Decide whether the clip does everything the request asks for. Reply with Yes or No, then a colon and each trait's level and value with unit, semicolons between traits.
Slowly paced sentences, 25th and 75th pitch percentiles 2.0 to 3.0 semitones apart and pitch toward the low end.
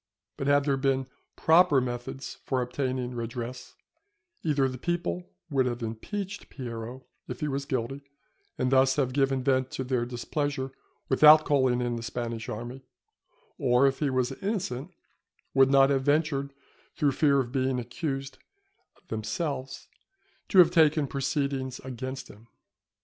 No: average, 145 wpm; narrow, 2.4 semitones; low, 130 Hz